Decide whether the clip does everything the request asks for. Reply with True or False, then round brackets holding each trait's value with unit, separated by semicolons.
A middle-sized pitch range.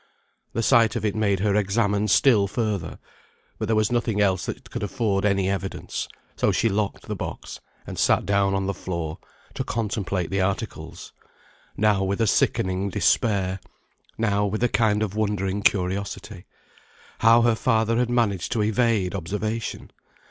False (2.3 semitones)